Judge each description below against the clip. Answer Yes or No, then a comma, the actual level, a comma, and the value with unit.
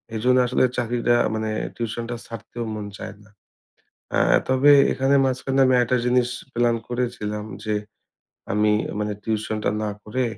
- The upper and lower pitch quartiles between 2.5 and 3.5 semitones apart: Yes, average, 2.8 semitones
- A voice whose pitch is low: Yes, low, 120 Hz